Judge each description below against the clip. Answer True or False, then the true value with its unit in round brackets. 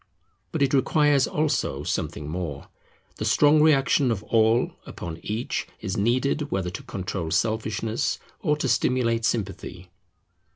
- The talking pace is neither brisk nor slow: False (130 wpm)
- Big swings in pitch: True (6.3 semitones)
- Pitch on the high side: False (115 Hz)